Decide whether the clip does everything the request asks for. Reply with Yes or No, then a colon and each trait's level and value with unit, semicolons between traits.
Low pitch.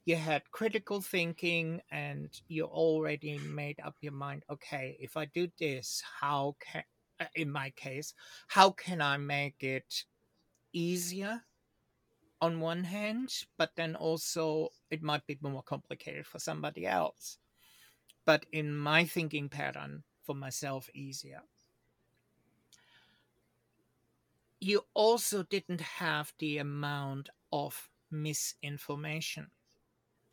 No: medium, 150 Hz